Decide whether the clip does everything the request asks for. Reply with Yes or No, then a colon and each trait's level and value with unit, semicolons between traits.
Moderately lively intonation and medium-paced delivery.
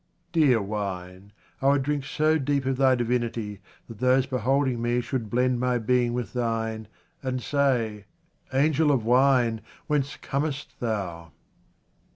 Yes: average, 3.3 semitones; average, 145 wpm